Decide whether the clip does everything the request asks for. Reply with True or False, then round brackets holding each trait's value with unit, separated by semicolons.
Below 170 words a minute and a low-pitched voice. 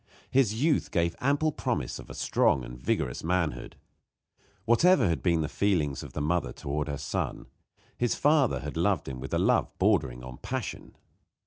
False (180 wpm; 85 Hz)